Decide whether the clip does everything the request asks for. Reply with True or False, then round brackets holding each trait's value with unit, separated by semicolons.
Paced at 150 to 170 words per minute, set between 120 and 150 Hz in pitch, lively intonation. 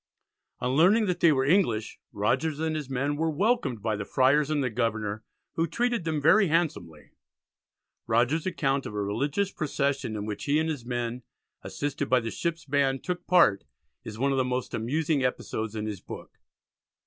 False (185 wpm; 140 Hz; 5.8 semitones)